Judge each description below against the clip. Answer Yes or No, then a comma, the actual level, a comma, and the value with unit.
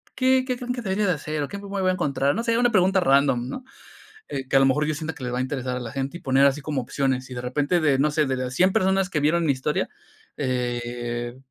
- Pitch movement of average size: No, wide, 6.0 semitones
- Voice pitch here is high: No, medium, 145 Hz